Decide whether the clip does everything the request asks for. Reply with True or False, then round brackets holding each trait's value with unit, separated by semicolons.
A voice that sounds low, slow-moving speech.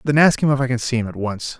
False (125 Hz; 375 wpm)